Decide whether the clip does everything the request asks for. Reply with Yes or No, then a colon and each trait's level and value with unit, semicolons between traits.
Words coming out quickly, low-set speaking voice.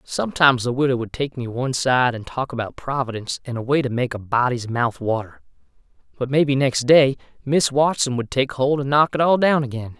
Yes: fast, 215 wpm; low, 130 Hz